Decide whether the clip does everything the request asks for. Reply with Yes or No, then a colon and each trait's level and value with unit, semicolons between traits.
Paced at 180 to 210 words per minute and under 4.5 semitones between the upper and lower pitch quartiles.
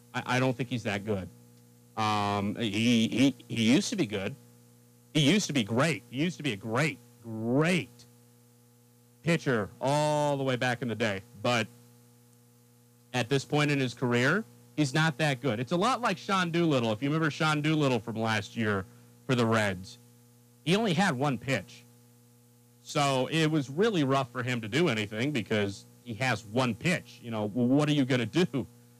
Yes: average, 190 wpm; average, 3.3 semitones